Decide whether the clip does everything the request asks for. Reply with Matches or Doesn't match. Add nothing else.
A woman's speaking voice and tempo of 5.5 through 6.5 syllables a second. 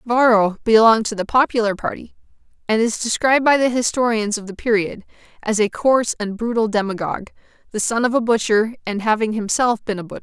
Matches